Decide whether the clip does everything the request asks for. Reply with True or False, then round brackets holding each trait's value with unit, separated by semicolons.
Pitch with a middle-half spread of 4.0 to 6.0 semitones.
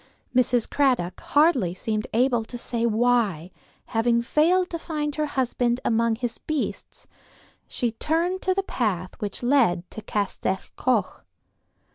True (4.9 semitones)